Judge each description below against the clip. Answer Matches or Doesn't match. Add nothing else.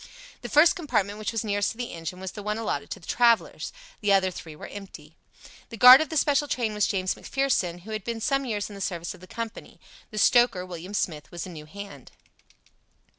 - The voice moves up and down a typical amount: Matches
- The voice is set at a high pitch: Matches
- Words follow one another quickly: Matches